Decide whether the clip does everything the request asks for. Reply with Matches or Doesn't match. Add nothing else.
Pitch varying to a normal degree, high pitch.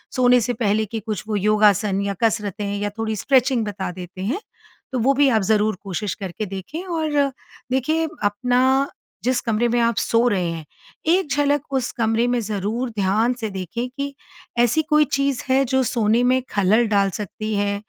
Matches